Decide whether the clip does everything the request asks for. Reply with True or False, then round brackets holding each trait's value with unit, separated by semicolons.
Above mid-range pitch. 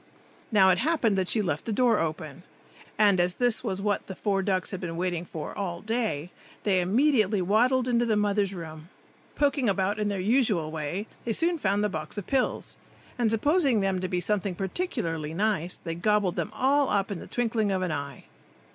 True (200 Hz)